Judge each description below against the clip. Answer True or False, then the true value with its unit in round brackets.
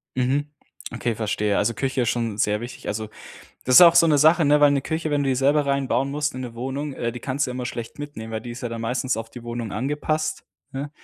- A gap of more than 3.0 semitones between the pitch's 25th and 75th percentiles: True (3.7 semitones)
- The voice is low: True (130 Hz)